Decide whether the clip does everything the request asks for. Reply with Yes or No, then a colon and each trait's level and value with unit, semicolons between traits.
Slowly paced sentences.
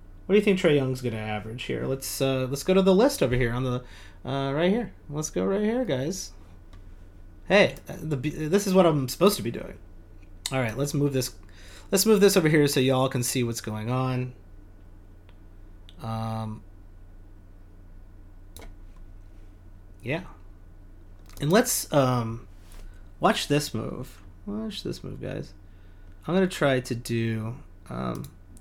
No: average, 155 wpm